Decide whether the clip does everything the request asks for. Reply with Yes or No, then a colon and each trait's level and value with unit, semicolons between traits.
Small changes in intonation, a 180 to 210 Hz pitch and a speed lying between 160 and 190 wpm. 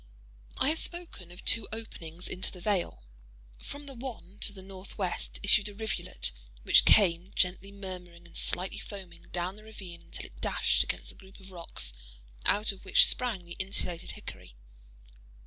No: average, 3.0 semitones; high, 190 Hz; average, 165 wpm